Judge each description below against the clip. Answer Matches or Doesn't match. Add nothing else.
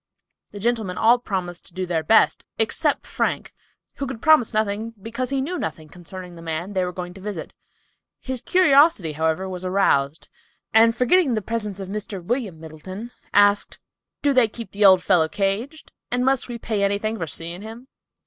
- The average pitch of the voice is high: Matches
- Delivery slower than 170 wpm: Doesn't match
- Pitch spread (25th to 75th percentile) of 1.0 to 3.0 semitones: Doesn't match